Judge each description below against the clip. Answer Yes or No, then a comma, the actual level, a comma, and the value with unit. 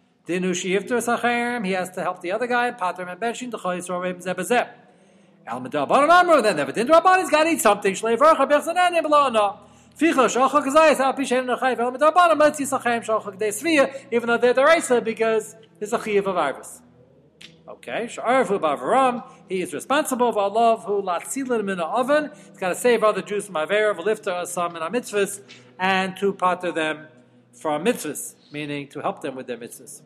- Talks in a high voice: Yes, high, 225 Hz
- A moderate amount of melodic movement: No, wide, 6.0 semitones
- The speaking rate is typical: No, slow, 105 wpm